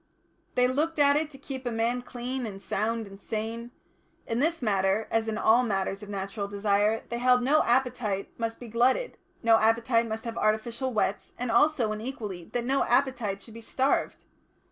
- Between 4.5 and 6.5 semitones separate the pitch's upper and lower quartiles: No, average, 2.9 semitones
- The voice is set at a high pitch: Yes, high, 230 Hz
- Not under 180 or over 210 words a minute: Yes, average, 190 wpm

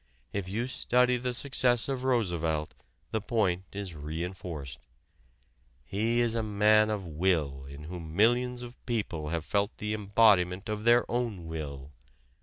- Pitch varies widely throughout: Yes, wide, 6.0 semitones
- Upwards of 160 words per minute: No, average, 150 wpm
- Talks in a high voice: No, low, 100 Hz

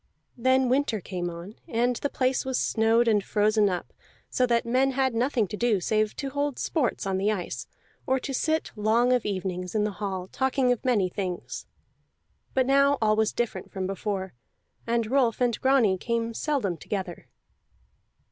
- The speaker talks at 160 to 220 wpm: Yes, average, 175 wpm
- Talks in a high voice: Yes, high, 230 Hz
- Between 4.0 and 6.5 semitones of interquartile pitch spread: Yes, average, 4.5 semitones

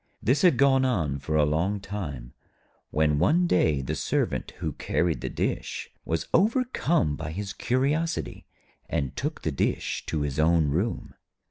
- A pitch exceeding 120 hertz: No, very low, 85 Hz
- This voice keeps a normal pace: Yes, average, 155 wpm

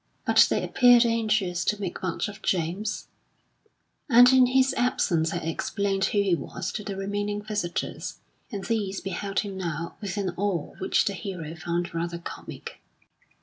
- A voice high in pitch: Yes, high, 195 Hz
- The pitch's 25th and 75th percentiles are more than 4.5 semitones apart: No, average, 3.4 semitones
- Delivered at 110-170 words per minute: Yes, average, 160 wpm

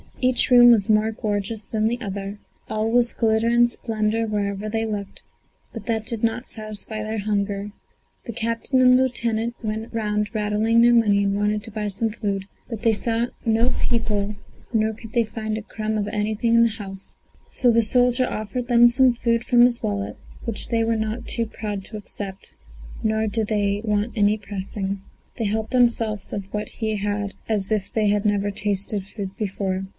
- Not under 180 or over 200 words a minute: Yes, average, 190 wpm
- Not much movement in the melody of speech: Yes, narrow, 2.0 semitones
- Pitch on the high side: Yes, high, 215 Hz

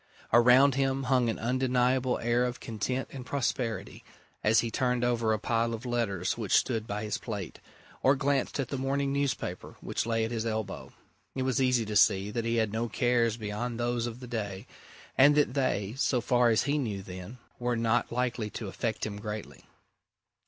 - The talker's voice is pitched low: Yes, low, 120 Hz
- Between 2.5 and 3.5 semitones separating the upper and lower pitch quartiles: Yes, average, 2.8 semitones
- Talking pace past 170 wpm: Yes, average, 190 wpm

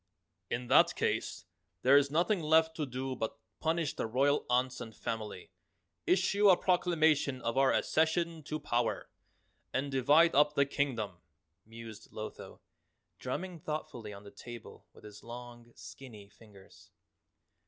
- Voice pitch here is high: No, low, 135 Hz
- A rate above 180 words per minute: No, average, 140 wpm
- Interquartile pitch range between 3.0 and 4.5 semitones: No, average, 5.3 semitones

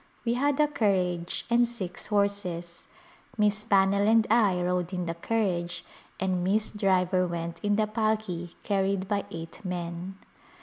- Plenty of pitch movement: No, average, 3.3 semitones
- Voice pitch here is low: No, high, 195 Hz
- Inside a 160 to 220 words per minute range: No, average, 145 wpm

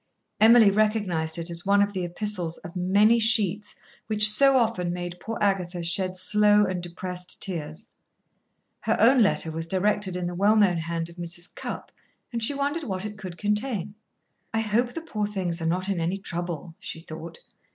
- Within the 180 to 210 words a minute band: Yes, average, 185 wpm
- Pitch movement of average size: Yes, average, 3.4 semitones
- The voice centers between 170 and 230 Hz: Yes, high, 190 Hz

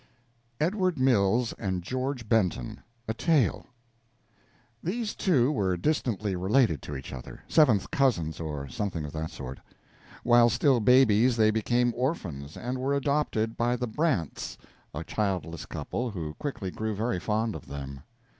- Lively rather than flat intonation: Yes, wide, 6.5 semitones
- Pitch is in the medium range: No, low, 110 Hz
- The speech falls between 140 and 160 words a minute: Yes, average, 145 wpm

